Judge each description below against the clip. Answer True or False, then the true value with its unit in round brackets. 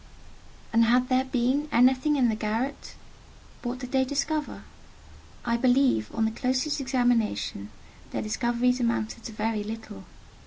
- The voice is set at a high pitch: True (245 Hz)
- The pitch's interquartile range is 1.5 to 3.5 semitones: True (2.7 semitones)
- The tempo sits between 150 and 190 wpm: False (140 wpm)